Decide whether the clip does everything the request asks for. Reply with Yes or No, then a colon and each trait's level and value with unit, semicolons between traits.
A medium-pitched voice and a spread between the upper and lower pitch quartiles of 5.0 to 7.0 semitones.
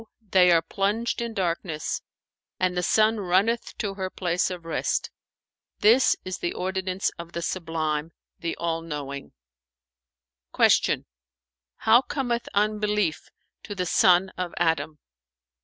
No: medium, 180 Hz; average, 4.0 semitones